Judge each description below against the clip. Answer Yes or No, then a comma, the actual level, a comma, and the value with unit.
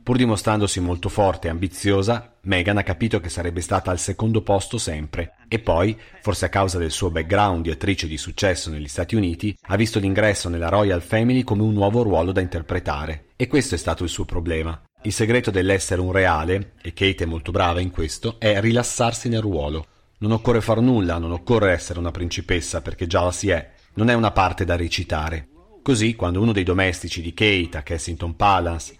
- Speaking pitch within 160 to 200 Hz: No, very low, 95 Hz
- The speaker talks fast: Yes, fast, 200 wpm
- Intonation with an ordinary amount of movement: Yes, average, 3.7 semitones